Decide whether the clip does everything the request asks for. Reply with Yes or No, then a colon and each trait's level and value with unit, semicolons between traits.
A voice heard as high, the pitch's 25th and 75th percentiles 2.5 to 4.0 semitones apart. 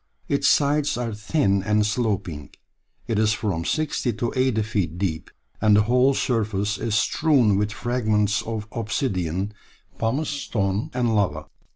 No: low, 110 Hz; average, 3.3 semitones